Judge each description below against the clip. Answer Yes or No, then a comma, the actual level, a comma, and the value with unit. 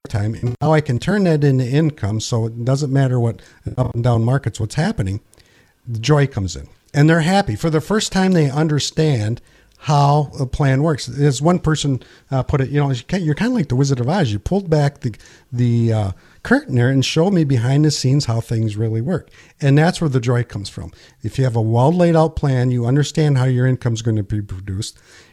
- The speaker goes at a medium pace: No, fast, 225 wpm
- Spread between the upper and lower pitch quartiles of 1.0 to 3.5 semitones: No, average, 4.9 semitones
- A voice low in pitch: Yes, low, 130 Hz